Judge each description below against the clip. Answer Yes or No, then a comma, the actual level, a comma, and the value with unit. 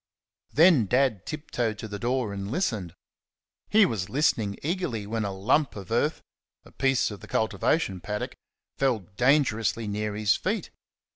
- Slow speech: No, average, 150 wpm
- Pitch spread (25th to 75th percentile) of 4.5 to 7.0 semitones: Yes, average, 4.9 semitones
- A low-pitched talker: Yes, low, 115 Hz